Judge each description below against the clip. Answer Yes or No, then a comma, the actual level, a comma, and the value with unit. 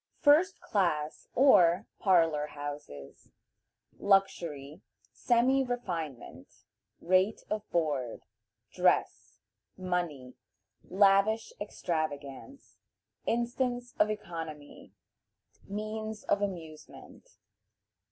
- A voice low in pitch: No, medium, 185 Hz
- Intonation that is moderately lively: No, wide, 6.2 semitones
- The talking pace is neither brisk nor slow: No, slow, 70 wpm